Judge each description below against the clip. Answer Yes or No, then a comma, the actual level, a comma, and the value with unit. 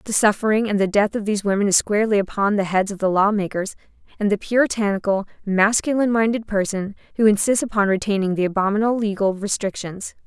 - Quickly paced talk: No, average, 175 wpm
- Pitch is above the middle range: Yes, high, 205 Hz